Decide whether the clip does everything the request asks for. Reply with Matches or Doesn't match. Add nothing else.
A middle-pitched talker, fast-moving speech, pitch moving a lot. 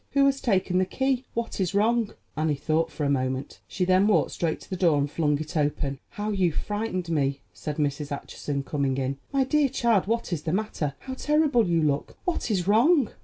Matches